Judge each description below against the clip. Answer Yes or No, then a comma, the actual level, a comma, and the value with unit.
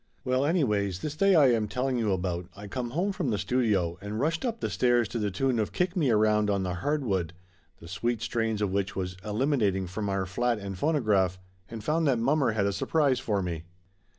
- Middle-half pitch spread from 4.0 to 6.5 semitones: Yes, wide, 5.5 semitones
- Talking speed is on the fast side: Yes, fast, 220 wpm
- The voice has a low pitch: Yes, low, 110 Hz